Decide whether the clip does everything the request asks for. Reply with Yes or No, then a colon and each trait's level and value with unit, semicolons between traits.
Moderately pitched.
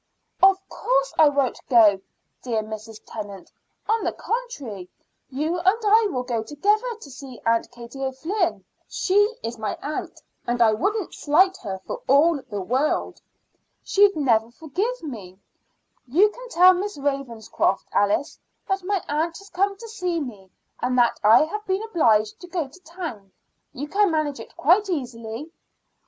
No: very high, 295 Hz